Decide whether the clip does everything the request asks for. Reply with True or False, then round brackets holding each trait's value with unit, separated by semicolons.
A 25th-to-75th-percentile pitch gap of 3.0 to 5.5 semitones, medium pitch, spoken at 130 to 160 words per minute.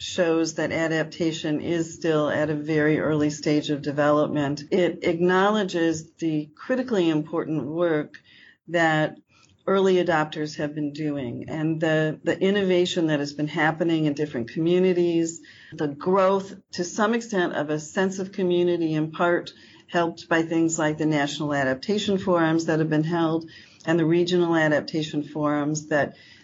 False (2.4 semitones; 160 Hz; 150 wpm)